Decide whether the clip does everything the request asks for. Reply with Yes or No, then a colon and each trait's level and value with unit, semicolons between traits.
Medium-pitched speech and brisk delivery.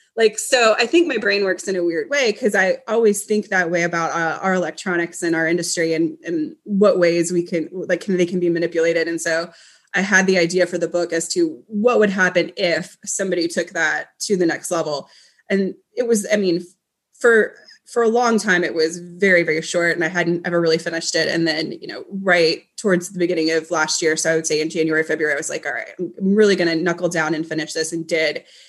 Yes: medium, 175 Hz; fast, 240 wpm